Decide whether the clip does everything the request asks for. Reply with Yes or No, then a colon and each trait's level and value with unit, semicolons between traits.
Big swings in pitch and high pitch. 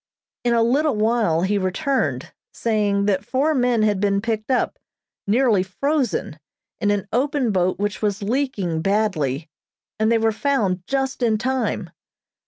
No: average, 4.3 semitones; high, 215 Hz